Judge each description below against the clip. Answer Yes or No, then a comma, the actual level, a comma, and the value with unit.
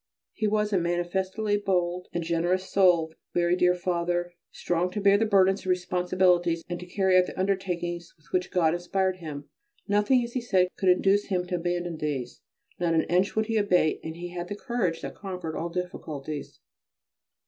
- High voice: No, medium, 180 Hz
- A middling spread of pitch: No, narrow, 1.9 semitones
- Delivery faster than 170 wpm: Yes, average, 180 wpm